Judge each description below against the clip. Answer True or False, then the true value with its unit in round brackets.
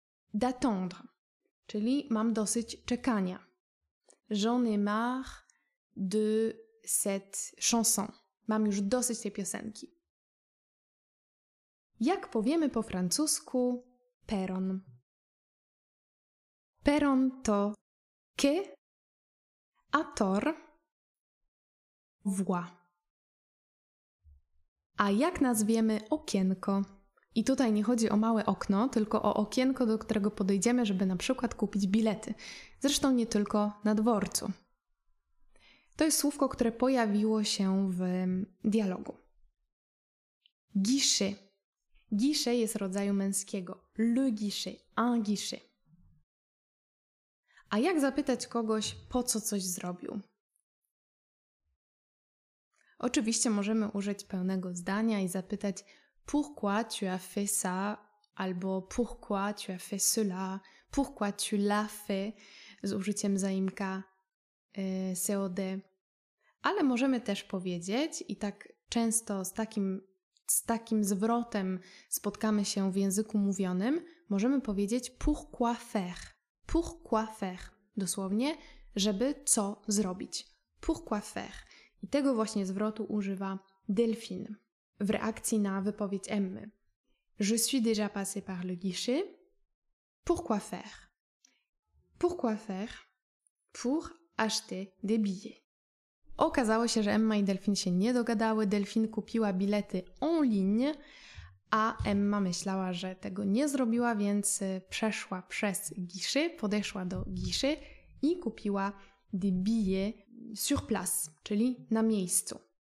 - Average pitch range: True (3.3 semitones)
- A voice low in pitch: False (210 Hz)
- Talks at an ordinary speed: False (105 wpm)